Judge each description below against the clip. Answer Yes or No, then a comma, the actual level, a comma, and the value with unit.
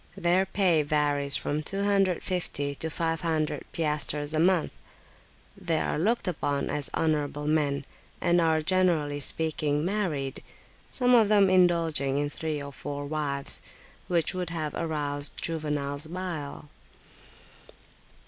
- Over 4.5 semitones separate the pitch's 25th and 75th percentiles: No, average, 3.4 semitones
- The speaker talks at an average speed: No, slow, 120 wpm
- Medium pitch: Yes, medium, 155 Hz